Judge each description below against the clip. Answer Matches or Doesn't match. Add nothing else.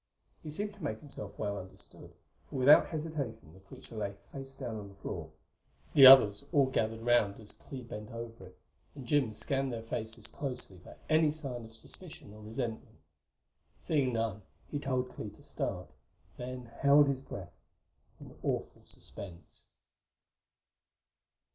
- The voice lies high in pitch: Doesn't match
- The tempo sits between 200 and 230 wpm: Doesn't match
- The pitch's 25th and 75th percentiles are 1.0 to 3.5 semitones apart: Doesn't match